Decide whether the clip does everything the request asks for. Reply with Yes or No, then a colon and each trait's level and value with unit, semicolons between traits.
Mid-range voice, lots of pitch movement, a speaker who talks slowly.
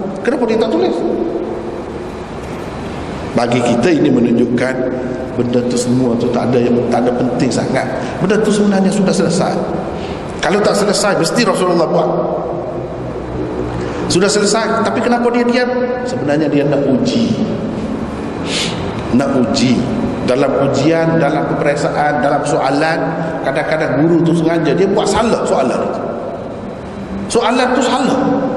No: medium, 160 Hz; wide, 8.9 semitones; average, 125 wpm